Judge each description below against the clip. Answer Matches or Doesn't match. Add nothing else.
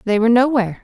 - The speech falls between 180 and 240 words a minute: Matches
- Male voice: Doesn't match